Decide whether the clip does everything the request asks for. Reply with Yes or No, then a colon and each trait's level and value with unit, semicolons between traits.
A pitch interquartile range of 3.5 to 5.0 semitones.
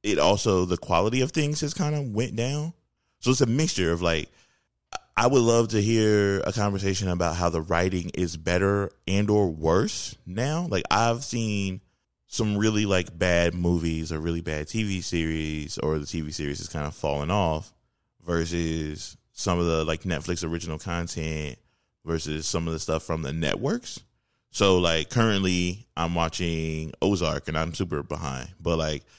Yes: average, 4.2 semitones